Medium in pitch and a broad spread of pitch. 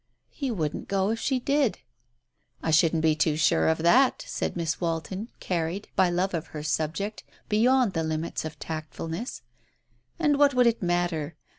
Yes: medium, 175 Hz; wide, 6.2 semitones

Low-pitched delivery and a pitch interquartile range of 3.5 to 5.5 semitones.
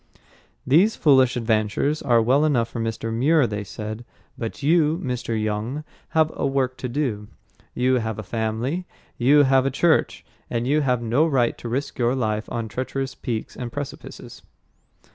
Yes: low, 125 Hz; average, 3.8 semitones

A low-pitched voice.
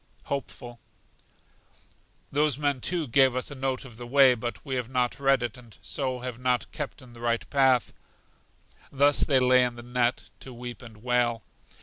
Yes: low, 125 Hz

